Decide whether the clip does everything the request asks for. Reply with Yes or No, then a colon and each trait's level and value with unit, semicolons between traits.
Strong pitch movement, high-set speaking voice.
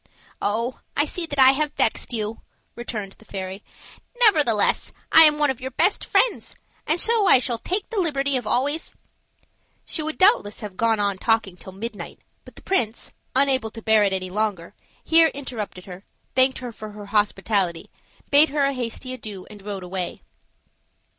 Yes: wide, 5.7 semitones; high, 230 Hz